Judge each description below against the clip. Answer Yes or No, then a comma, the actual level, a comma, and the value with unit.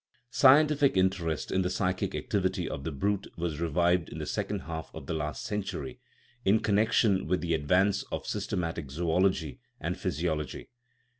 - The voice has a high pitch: No, very low, 90 Hz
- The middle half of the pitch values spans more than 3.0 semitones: Yes, average, 3.6 semitones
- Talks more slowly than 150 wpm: No, average, 155 wpm